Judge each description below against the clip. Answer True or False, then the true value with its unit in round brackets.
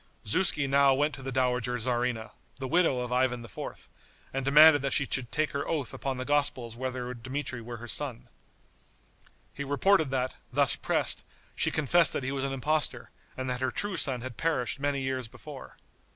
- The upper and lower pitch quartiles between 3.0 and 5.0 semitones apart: False (2.4 semitones)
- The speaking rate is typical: True (185 wpm)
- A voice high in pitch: False (130 Hz)